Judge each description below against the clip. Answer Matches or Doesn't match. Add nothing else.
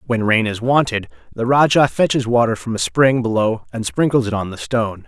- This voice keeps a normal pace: Doesn't match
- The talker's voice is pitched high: Doesn't match